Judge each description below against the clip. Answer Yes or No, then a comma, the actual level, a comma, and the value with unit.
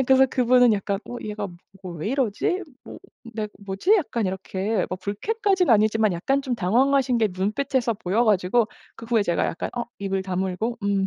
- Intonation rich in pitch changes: No, average, 4.4 semitones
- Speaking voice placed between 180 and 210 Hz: No, high, 220 Hz